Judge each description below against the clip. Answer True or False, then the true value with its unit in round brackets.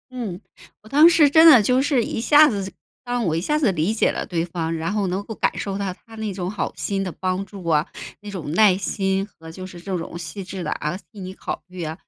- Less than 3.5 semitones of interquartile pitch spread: False (3.8 semitones)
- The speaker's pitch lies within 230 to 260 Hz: False (195 Hz)